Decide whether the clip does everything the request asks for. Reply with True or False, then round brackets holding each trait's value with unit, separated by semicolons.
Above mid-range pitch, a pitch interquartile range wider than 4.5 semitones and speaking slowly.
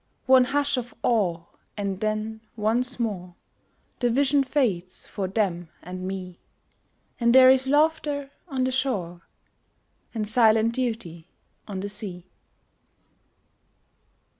True (220 Hz; 5.4 semitones; 115 wpm)